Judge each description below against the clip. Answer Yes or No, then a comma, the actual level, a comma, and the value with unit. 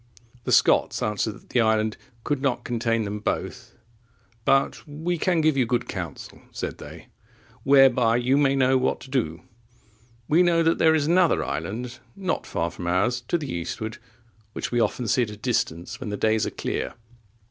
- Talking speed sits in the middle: Yes, average, 180 wpm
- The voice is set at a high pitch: No, low, 125 Hz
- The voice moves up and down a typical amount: Yes, average, 4.8 semitones